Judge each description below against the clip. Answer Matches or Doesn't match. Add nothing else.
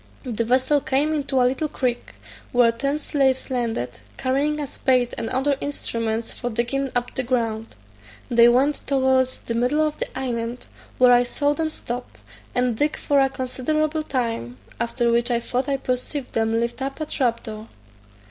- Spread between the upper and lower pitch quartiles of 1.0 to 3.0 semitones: Matches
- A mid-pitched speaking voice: Doesn't match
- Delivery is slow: Doesn't match